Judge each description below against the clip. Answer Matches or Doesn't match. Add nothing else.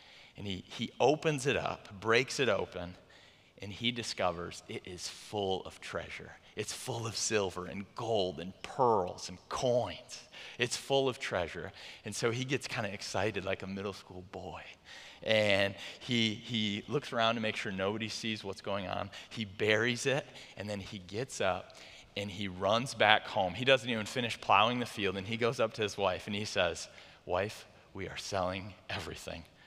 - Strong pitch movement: Doesn't match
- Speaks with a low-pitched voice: Matches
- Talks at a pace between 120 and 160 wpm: Doesn't match